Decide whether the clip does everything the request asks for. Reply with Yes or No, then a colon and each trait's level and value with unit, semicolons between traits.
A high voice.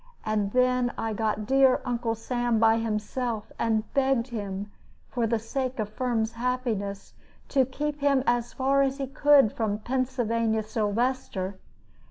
Yes: high, 235 Hz